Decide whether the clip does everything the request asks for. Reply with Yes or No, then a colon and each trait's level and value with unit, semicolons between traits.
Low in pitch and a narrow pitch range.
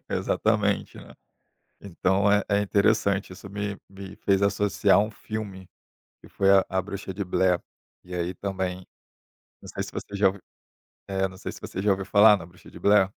Yes: low, 100 Hz; narrow, 1.4 semitones